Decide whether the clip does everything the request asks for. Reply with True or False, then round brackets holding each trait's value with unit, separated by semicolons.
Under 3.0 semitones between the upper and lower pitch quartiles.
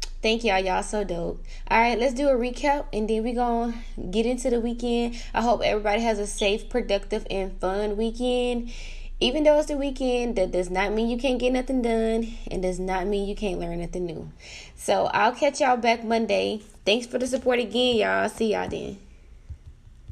False (3.5 semitones)